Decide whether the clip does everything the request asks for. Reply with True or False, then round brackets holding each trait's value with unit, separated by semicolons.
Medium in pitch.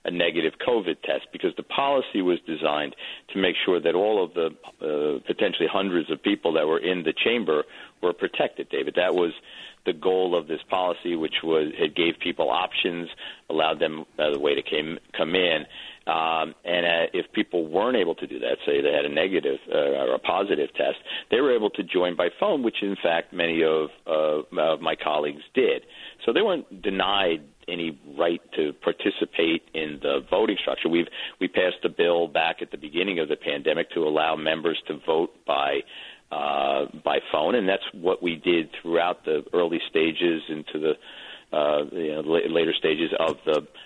False (85 Hz)